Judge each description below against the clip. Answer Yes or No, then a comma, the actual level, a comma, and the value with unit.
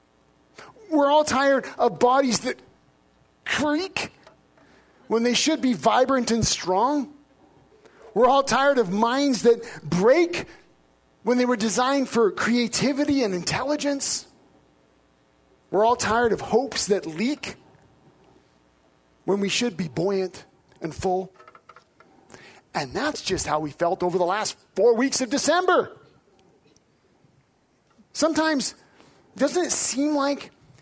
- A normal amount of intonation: No, wide, 7.2 semitones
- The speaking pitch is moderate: No, high, 240 Hz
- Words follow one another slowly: Yes, slow, 120 wpm